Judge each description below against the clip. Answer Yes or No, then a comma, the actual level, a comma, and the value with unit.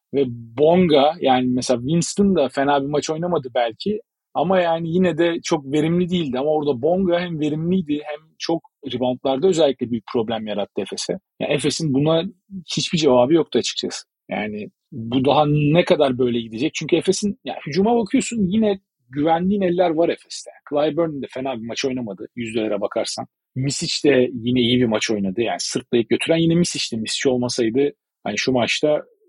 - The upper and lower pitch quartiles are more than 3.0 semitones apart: Yes, average, 5.2 semitones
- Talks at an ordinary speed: No, fast, 165 wpm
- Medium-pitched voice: Yes, medium, 150 Hz